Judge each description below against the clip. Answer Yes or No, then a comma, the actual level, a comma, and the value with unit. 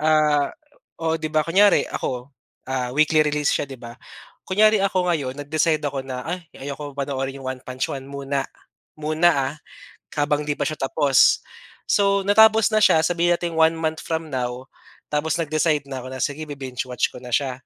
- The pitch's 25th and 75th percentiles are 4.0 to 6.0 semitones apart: No, average, 3.3 semitones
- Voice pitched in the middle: Yes, medium, 150 Hz